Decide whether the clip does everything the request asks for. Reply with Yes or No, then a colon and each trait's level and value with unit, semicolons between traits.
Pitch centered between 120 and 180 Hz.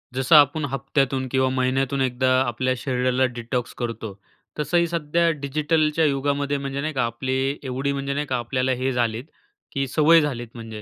Yes: low, 135 Hz